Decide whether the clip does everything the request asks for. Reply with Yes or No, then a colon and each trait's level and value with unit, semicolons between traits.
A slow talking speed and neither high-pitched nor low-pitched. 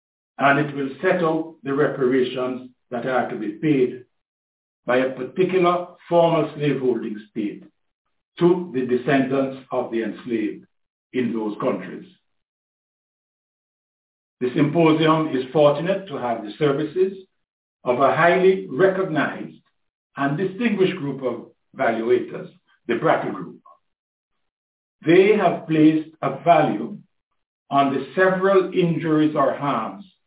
Yes: slow, 115 wpm; medium, 150 Hz